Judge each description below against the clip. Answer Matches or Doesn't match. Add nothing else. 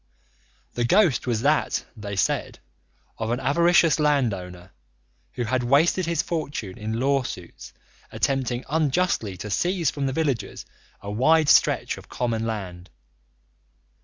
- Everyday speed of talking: Doesn't match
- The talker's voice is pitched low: Matches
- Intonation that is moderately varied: Doesn't match